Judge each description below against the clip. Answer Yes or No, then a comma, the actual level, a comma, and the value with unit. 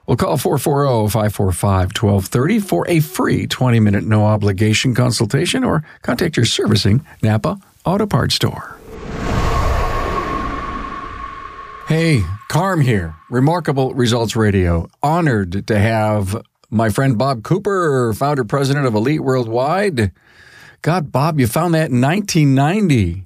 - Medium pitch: No, low, 130 Hz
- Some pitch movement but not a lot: No, wide, 6.4 semitones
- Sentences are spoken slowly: Yes, slow, 110 wpm